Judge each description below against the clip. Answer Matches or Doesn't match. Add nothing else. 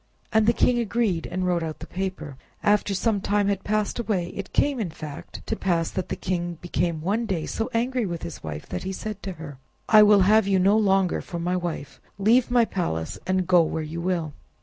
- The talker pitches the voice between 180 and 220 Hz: Matches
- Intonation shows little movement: Doesn't match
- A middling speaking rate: Doesn't match